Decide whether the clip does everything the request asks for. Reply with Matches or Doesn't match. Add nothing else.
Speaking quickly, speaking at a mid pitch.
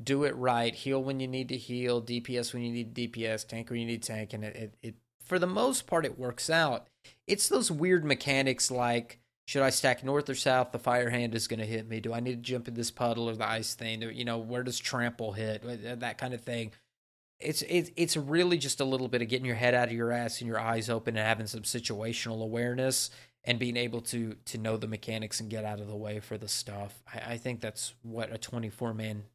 Doesn't match